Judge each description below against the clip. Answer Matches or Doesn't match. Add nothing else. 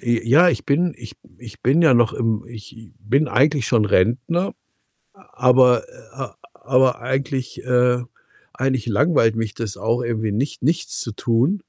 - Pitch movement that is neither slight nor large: Matches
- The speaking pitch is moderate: Doesn't match